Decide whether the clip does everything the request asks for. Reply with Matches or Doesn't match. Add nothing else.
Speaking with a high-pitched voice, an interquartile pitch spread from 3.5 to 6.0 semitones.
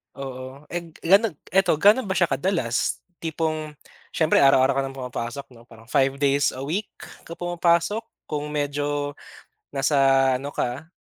Doesn't match